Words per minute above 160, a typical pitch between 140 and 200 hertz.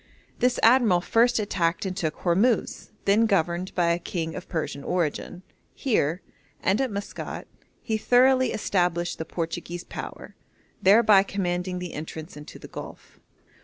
No: average, 140 wpm; medium, 185 Hz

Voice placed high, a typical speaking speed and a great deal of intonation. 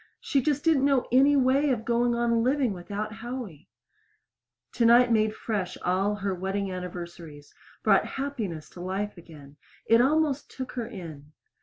Yes: high, 220 Hz; average, 150 wpm; wide, 5.9 semitones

